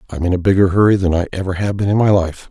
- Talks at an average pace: No, fast, 310 wpm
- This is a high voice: No, very low, 95 Hz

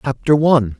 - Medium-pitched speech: No, low, 130 Hz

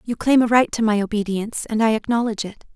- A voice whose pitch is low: No, high, 220 Hz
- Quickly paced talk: Yes, fast, 240 wpm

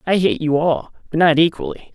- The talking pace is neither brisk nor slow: No, fast, 215 wpm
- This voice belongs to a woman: No, male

